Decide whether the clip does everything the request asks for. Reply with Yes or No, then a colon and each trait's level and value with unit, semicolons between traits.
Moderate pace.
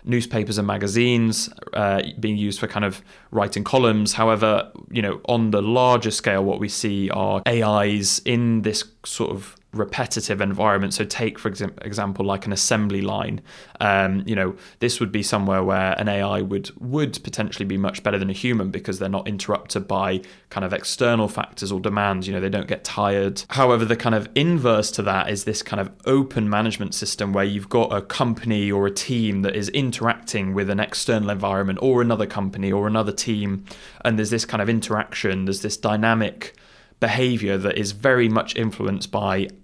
Yes: average, 190 wpm